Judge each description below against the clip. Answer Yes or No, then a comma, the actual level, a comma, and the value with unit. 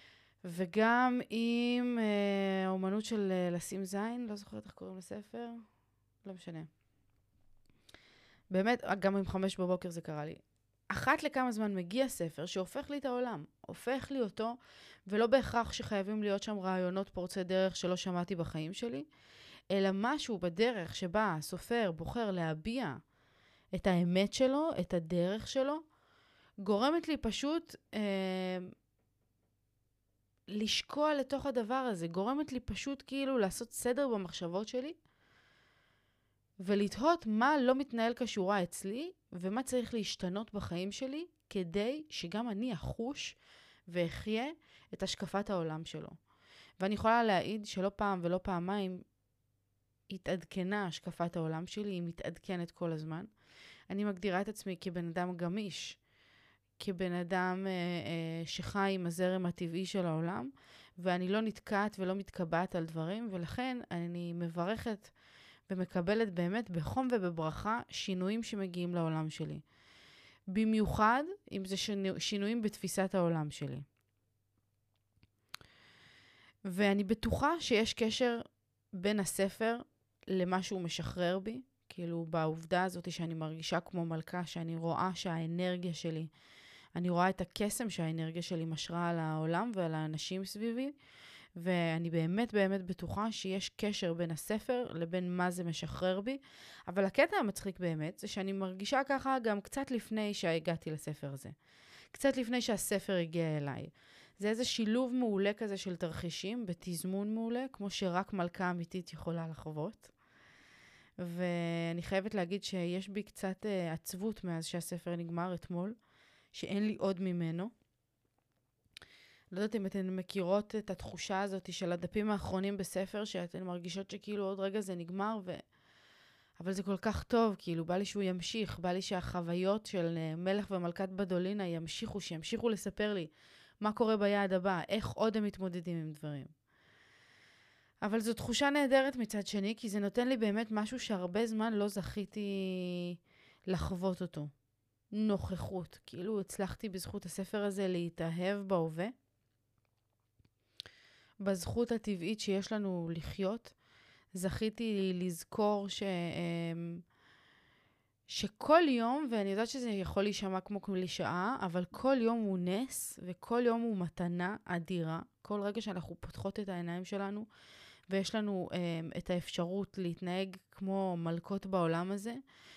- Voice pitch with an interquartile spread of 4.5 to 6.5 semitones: No, average, 3.8 semitones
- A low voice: No, high, 190 Hz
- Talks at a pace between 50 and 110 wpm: No, average, 130 wpm